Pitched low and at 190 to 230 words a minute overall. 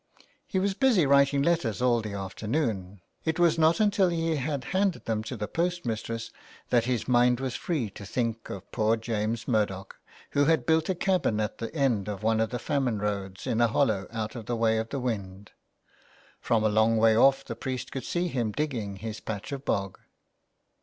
Yes: low, 115 Hz; average, 200 wpm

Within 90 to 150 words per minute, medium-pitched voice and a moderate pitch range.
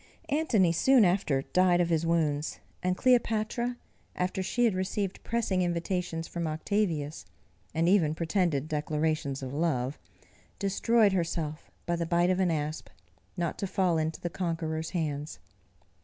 Yes: average, 140 wpm; medium, 170 Hz; average, 3.3 semitones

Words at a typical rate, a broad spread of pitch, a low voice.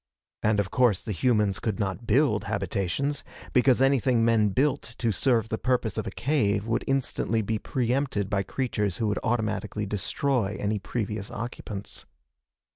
No: average, 155 wpm; average, 3.6 semitones; low, 110 Hz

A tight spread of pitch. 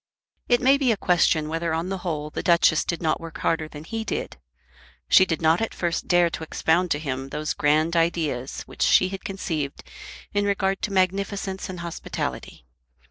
No: average, 3.4 semitones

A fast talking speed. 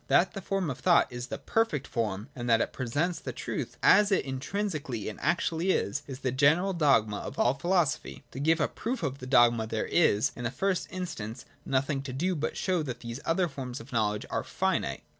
Yes: fast, 215 wpm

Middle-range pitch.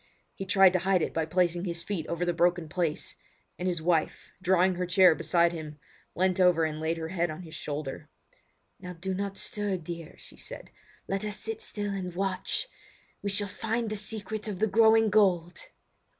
Yes: medium, 180 Hz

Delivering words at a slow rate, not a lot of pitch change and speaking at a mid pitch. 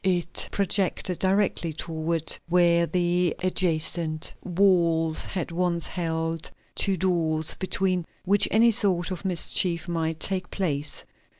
Yes: slow, 115 wpm; narrow, 2.3 semitones; medium, 175 Hz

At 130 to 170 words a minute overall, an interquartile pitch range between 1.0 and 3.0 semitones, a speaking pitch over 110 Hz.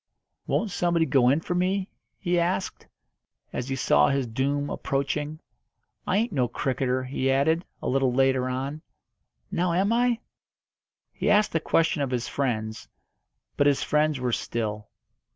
No: average, 150 wpm; average, 4.9 semitones; medium, 140 Hz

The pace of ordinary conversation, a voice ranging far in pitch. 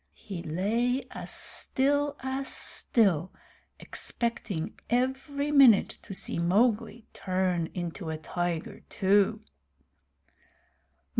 No: slow, 90 wpm; wide, 6.8 semitones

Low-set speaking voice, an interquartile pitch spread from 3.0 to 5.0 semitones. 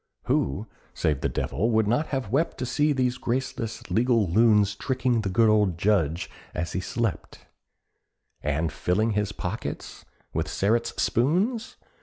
Yes: low, 110 Hz; average, 4.5 semitones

